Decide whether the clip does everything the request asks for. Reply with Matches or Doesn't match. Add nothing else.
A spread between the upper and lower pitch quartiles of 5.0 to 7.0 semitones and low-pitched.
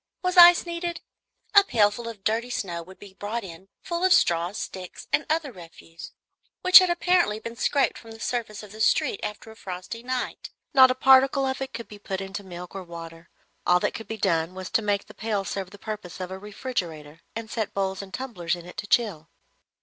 Doesn't match